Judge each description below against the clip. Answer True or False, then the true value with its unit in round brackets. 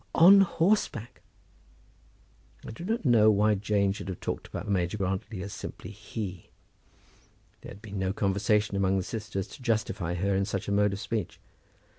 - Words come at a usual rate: True (170 wpm)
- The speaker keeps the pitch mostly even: True (2.2 semitones)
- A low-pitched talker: True (105 Hz)